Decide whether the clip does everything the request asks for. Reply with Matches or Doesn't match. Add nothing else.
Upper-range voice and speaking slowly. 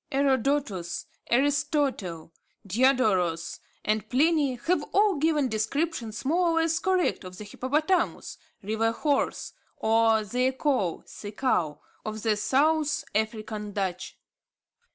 Matches